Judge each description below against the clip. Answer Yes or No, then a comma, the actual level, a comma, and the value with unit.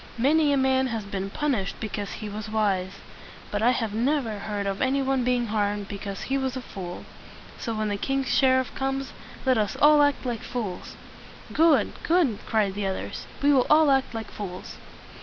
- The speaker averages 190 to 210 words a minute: Yes, average, 195 wpm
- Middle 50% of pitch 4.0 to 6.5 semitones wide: Yes, average, 4.8 semitones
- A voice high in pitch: Yes, high, 230 Hz